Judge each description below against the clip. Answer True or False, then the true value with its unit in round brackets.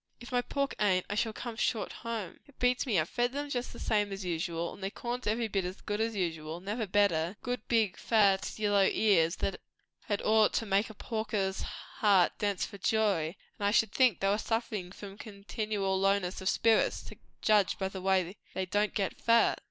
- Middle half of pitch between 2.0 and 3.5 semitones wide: True (2.8 semitones)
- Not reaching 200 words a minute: False (205 wpm)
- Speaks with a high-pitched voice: True (205 Hz)